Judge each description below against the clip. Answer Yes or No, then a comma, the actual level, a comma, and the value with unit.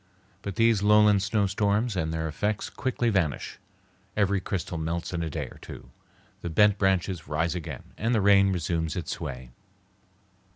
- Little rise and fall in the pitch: No, average, 4.0 semitones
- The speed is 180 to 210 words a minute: No, average, 160 wpm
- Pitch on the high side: No, very low, 95 Hz